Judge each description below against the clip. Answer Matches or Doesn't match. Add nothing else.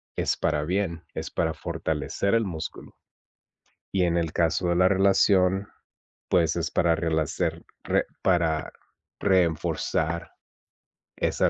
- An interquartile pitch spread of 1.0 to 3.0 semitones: Matches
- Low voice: Matches